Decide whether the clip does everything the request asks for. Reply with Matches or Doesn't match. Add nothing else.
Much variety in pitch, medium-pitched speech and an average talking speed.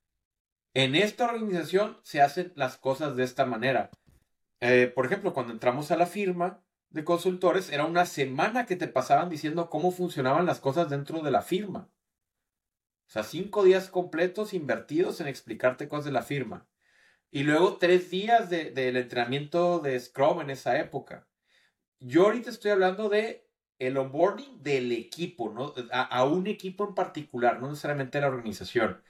Matches